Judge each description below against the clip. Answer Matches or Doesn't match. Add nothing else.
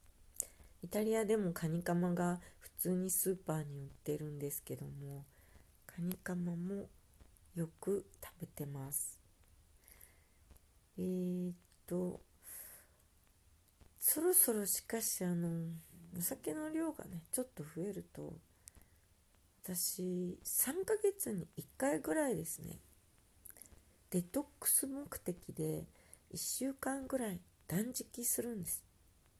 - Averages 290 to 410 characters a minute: Doesn't match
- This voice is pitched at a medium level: Matches